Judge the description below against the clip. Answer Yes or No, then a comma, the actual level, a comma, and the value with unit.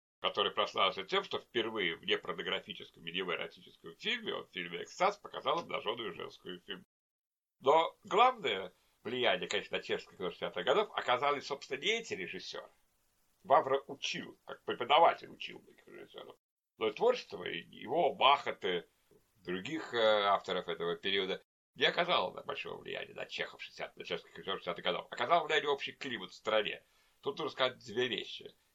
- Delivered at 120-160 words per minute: Yes, average, 155 wpm